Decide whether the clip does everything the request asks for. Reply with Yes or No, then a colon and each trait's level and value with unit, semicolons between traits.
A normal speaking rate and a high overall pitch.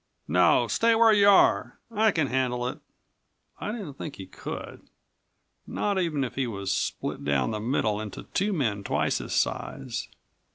No: average, 165 wpm; low, 135 Hz